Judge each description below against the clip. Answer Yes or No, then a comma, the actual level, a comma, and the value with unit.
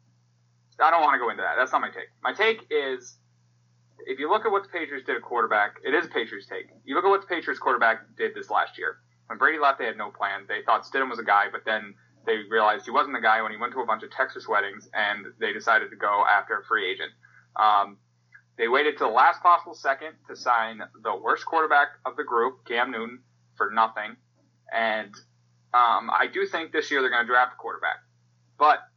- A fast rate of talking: Yes, fast, 235 wpm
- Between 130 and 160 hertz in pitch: No, low, 115 Hz